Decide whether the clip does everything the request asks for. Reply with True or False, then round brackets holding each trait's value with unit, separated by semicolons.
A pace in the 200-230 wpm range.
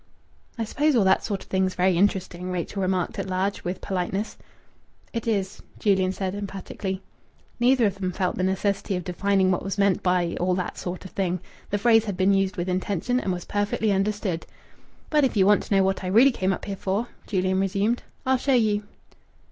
True (205 wpm)